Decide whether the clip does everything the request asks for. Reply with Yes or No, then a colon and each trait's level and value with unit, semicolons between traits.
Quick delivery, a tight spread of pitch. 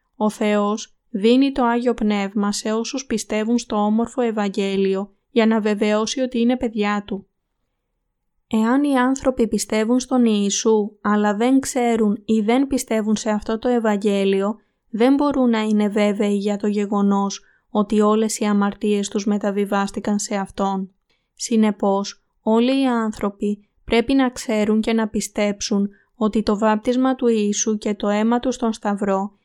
No: average, 145 wpm; narrow, 2.2 semitones